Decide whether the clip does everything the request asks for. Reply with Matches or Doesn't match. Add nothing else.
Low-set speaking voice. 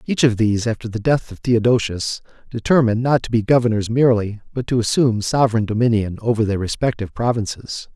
Matches